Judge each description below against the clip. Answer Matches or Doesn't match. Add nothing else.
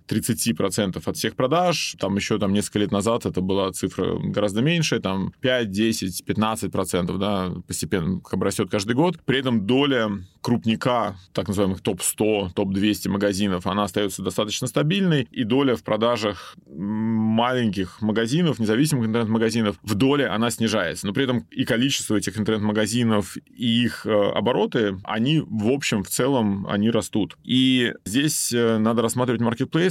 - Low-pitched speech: Matches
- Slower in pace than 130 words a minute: Doesn't match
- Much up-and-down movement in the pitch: Doesn't match